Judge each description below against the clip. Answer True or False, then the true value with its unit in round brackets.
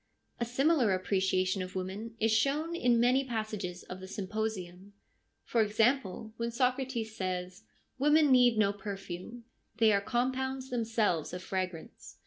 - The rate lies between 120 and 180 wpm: True (140 wpm)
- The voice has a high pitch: True (220 Hz)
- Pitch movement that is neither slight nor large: True (4.7 semitones)